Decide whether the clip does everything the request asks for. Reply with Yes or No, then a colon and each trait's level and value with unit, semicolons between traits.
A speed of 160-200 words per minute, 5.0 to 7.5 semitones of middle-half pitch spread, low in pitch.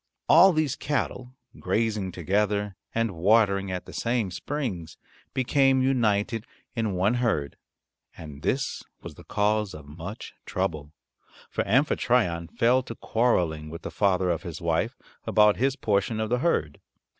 No: average, 145 wpm; wide, 5.6 semitones; low, 105 Hz